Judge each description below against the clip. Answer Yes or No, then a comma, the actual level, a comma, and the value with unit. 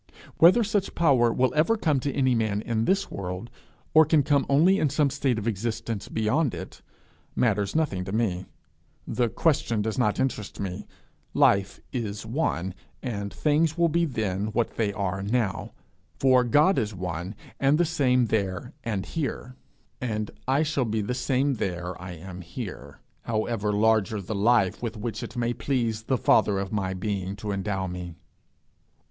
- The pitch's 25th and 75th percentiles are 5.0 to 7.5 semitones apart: Yes, average, 5.3 semitones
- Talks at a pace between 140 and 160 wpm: No, average, 170 wpm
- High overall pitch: No, low, 115 Hz